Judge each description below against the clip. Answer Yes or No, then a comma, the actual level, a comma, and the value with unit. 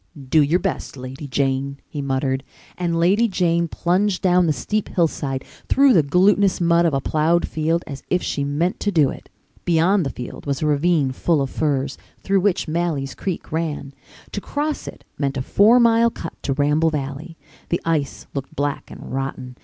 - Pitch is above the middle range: No, medium, 160 Hz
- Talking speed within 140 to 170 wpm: No, average, 185 wpm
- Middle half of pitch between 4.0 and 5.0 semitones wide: Yes, average, 4.4 semitones